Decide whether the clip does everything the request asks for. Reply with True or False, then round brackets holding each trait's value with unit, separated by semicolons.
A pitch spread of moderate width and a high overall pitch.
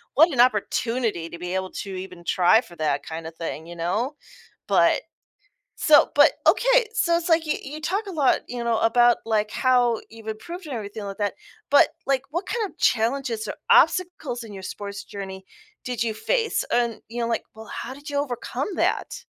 False (6.2 semitones; 235 Hz)